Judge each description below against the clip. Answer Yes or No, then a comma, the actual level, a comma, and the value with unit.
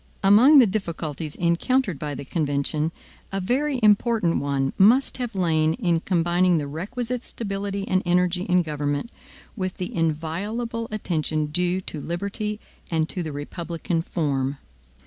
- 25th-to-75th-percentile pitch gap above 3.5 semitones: Yes, average, 4.8 semitones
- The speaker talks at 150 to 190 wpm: No, average, 140 wpm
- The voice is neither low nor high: Yes, medium, 180 Hz